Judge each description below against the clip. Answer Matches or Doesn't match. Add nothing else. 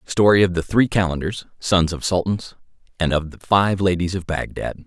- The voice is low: Matches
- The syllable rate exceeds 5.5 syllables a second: Doesn't match